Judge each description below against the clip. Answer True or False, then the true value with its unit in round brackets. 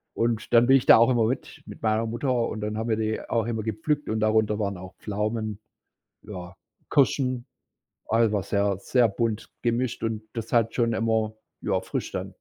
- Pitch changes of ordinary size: False (1.7 semitones)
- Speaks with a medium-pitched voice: False (110 Hz)